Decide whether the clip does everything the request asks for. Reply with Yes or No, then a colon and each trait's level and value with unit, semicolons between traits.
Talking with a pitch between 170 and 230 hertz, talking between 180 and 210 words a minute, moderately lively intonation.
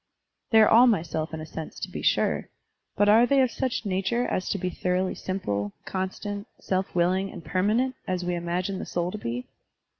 Yes: medium, 185 Hz; fast, 205 wpm; average, 3.0 semitones